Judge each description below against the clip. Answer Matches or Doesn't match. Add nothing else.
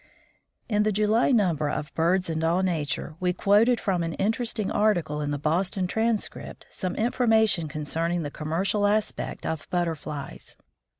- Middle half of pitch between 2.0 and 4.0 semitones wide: Doesn't match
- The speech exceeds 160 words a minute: Doesn't match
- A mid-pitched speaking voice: Matches